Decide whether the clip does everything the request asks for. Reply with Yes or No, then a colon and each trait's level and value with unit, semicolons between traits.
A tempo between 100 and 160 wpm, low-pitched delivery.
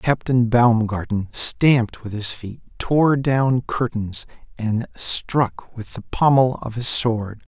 Yes: slow, 135 wpm; low, 120 Hz